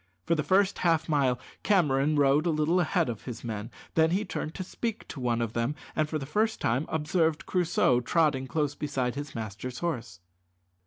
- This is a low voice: No, medium, 150 Hz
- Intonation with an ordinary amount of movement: Yes, average, 4.9 semitones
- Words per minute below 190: No, average, 195 wpm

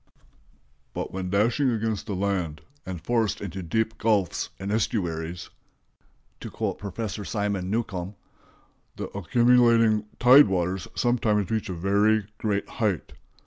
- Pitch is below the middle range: Yes, low, 105 Hz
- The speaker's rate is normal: No, slow, 125 wpm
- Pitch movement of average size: Yes, average, 3.1 semitones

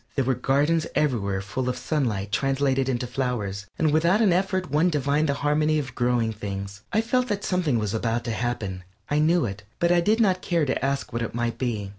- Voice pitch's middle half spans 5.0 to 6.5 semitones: Yes, wide, 5.5 semitones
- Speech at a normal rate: No, fast, 215 wpm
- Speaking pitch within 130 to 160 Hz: Yes, low, 135 Hz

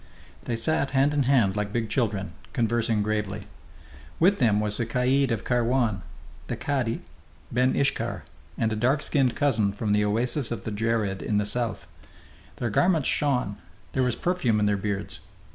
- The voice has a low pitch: Yes, low, 115 Hz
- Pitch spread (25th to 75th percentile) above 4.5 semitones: No, average, 3.8 semitones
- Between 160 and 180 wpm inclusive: Yes, average, 170 wpm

